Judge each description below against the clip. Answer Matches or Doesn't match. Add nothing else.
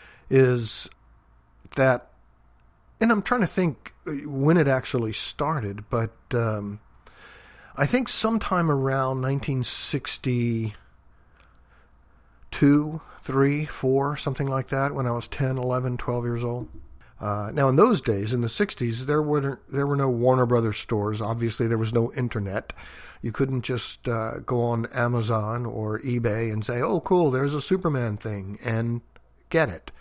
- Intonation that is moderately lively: Matches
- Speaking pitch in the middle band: Doesn't match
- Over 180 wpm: Doesn't match